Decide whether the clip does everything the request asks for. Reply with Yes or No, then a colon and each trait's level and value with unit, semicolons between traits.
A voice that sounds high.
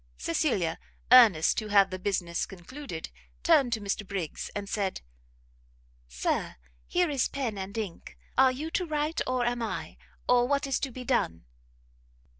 Yes: high, 225 Hz